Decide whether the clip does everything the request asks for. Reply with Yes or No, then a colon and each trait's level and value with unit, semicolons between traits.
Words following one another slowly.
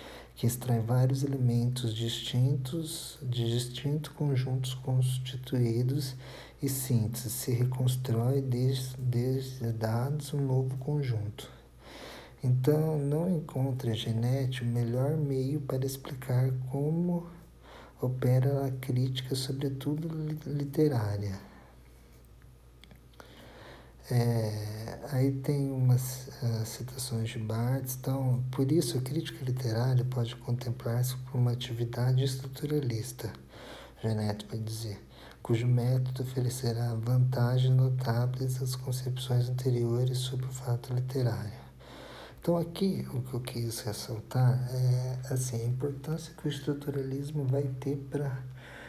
Yes: slow, 105 wpm